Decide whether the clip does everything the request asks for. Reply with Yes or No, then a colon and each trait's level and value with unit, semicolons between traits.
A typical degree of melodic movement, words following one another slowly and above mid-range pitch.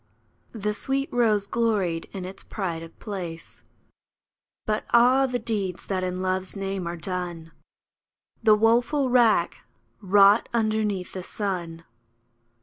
Yes: average, 3.7 semitones; slow, 125 wpm; high, 200 Hz